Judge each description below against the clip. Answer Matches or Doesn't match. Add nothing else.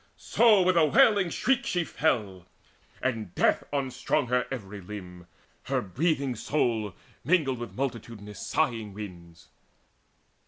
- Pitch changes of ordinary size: Doesn't match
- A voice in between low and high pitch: Doesn't match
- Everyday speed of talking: Doesn't match